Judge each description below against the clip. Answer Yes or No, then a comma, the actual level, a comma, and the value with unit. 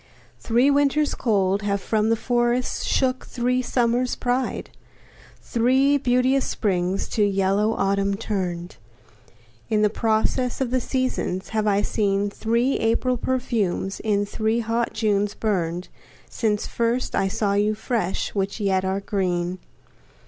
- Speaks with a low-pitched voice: No, high, 220 Hz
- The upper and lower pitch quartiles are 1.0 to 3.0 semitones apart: No, average, 3.8 semitones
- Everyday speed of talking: No, slow, 130 wpm